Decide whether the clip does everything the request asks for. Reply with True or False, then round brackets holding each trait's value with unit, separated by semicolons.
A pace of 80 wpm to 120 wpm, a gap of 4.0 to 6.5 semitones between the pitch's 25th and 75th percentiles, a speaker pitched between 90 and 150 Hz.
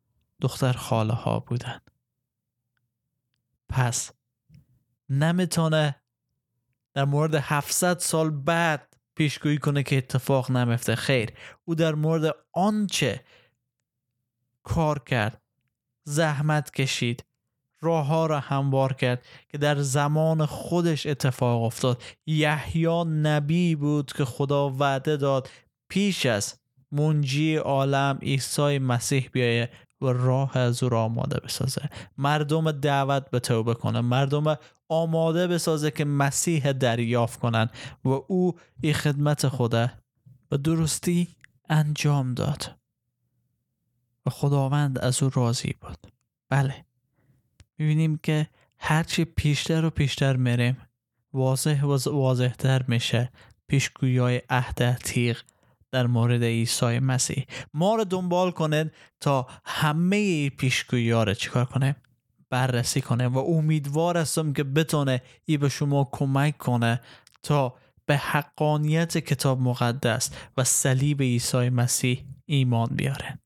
False (110 wpm; 3.4 semitones; 135 Hz)